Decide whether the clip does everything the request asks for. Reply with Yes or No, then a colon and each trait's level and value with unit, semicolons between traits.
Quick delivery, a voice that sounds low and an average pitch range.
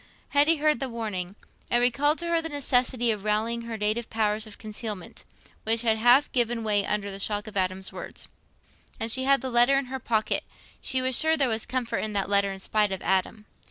No: fast, 215 wpm; high, 230 Hz; average, 3.6 semitones